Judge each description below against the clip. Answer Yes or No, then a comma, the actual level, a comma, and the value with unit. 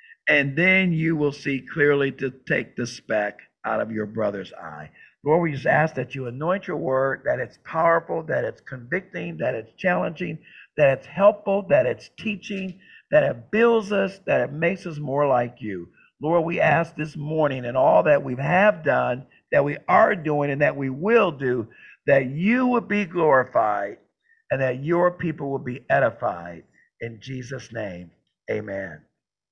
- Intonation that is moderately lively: No, wide, 6.1 semitones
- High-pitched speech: No, medium, 150 Hz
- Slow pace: No, average, 175 wpm